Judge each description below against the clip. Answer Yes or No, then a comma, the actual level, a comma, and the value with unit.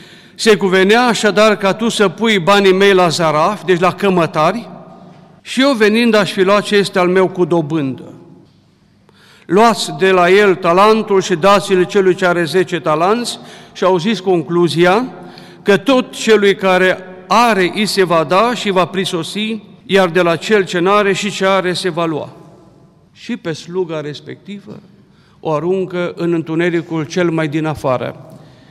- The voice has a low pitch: No, medium, 185 Hz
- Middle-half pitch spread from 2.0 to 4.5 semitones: Yes, average, 2.9 semitones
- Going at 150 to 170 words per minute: Yes, average, 165 wpm